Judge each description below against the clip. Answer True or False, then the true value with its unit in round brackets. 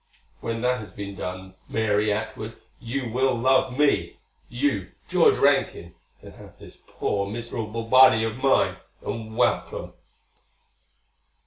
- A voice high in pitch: False (115 Hz)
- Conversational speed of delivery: False (125 wpm)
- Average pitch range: True (3.3 semitones)